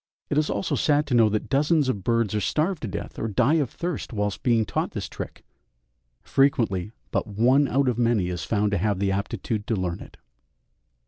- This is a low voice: Yes, low, 115 Hz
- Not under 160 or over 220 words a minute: Yes, fast, 205 wpm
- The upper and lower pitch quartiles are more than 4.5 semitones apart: Yes, average, 5.3 semitones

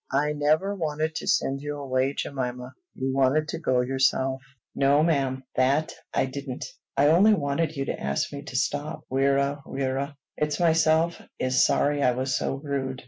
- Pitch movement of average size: No, narrow, 2.3 semitones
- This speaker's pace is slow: No, average, 170 wpm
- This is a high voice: No, medium, 140 Hz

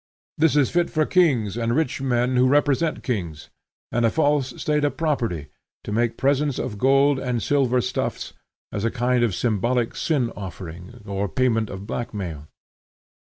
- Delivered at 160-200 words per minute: Yes, average, 165 wpm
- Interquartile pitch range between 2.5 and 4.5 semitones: No, average, 5.0 semitones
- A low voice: Yes, low, 125 Hz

